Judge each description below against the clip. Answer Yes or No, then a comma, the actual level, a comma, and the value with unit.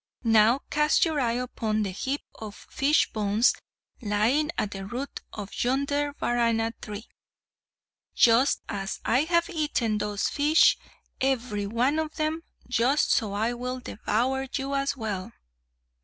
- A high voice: Yes, high, 245 Hz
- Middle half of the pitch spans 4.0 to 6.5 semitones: Yes, average, 4.7 semitones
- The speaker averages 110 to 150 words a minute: Yes, average, 140 wpm